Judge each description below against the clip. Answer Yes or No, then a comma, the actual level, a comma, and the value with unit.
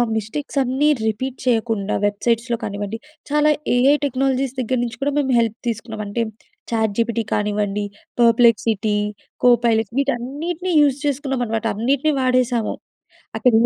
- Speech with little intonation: No, average, 3.4 semitones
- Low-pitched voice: No, high, 235 Hz